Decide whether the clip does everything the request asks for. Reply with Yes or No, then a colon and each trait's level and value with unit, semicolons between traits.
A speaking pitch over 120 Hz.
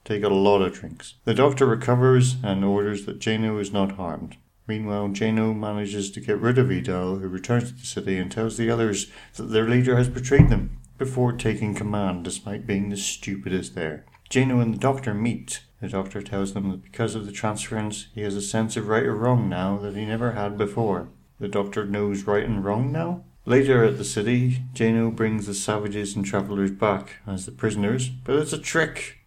No: low, 105 Hz